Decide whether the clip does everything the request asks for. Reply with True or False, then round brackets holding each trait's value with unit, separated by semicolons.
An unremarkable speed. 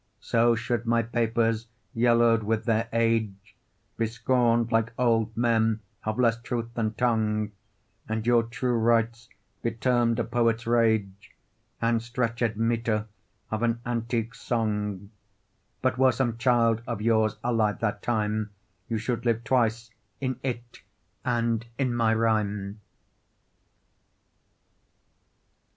False (120 wpm)